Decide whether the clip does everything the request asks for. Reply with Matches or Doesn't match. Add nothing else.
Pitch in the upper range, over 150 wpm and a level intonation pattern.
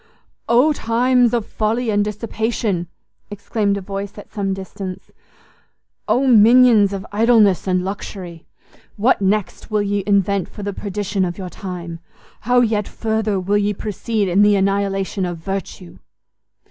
Doesn't match